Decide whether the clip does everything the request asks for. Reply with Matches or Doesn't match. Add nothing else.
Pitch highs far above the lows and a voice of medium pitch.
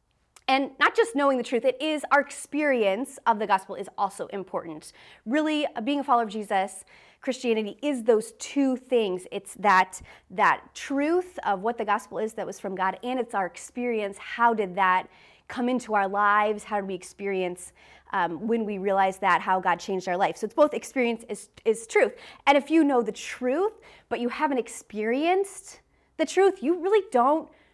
Doesn't match